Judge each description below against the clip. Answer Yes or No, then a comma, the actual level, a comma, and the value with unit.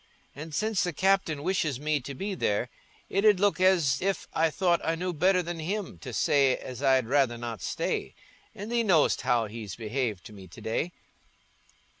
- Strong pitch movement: Yes, wide, 6.8 semitones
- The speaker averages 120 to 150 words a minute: No, average, 190 wpm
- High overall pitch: No, medium, 155 Hz